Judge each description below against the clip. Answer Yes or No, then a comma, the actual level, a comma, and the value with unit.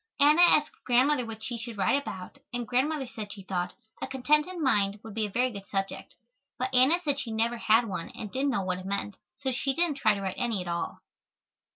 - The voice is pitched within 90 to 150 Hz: No, high, 240 Hz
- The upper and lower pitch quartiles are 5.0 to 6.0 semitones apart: Yes, wide, 5.4 semitones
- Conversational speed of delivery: No, fast, 225 wpm